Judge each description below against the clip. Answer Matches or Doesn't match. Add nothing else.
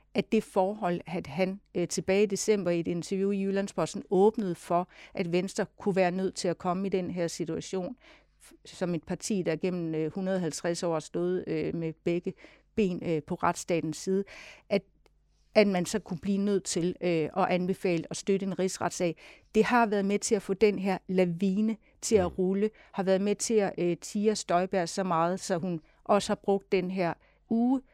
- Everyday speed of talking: Matches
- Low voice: Doesn't match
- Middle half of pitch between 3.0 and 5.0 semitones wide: Doesn't match